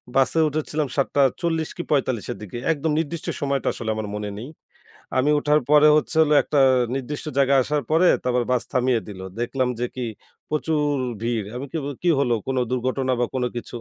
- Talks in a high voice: No, low, 135 Hz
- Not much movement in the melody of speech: No, average, 3.4 semitones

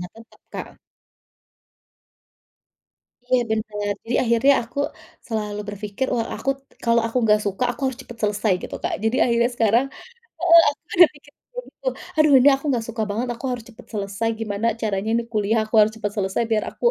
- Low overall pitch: No, high, 225 Hz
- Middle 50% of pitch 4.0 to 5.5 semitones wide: No, average, 3.0 semitones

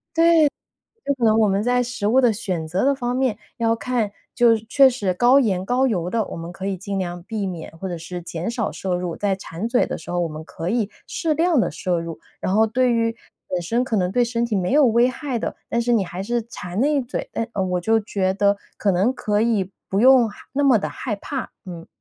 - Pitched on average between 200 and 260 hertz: Yes, high, 220 Hz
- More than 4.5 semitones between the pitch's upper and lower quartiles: Yes, average, 4.9 semitones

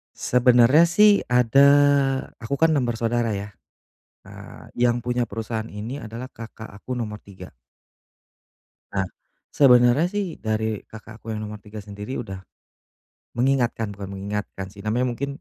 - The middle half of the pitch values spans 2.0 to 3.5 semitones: Yes, average, 2.8 semitones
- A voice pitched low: Yes, low, 115 Hz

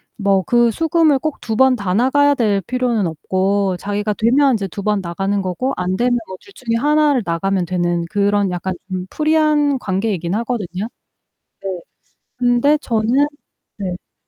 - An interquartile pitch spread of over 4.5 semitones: Yes, average, 5.2 semitones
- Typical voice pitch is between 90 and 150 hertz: No, high, 210 Hz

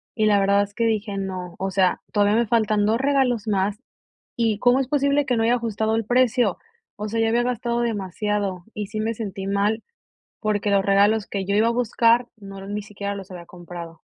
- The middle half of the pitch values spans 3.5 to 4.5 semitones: No, average, 2.7 semitones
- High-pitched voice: Yes, high, 210 Hz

